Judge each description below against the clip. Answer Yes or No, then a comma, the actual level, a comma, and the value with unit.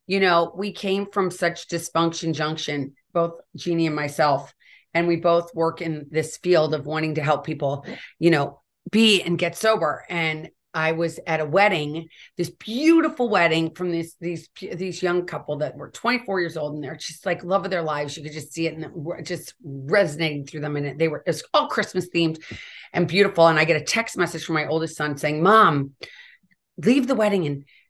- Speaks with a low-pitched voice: No, medium, 165 Hz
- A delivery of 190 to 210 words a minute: Yes, average, 200 wpm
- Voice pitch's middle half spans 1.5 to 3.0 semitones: Yes, average, 2.7 semitones